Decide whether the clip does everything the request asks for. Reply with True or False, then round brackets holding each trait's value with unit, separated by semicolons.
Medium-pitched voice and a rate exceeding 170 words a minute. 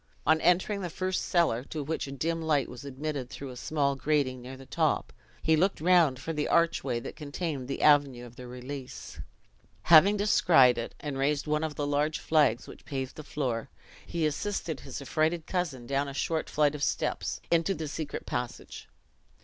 True (145 Hz; 190 wpm)